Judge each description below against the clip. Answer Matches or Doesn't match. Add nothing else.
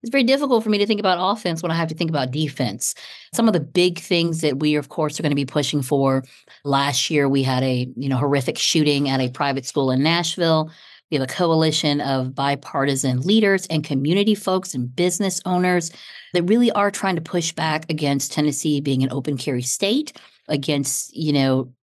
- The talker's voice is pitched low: Doesn't match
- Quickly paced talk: Matches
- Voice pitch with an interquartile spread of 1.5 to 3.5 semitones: Doesn't match